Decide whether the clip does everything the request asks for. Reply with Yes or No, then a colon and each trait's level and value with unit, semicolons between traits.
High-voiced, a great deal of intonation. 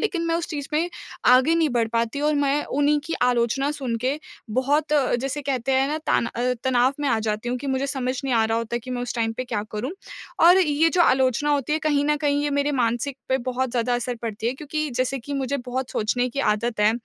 No: very high, 260 Hz; average, 3.2 semitones